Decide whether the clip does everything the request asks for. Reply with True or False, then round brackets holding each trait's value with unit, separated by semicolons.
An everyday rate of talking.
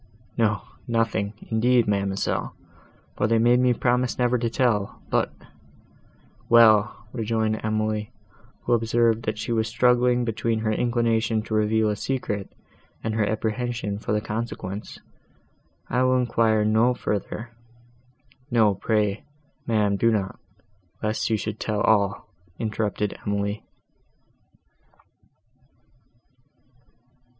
False (110 wpm)